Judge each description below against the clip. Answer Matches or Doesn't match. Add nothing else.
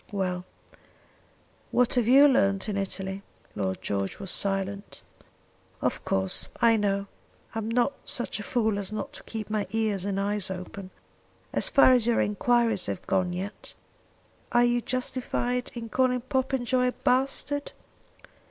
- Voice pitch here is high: Matches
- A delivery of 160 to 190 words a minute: Doesn't match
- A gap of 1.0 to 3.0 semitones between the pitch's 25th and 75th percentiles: Doesn't match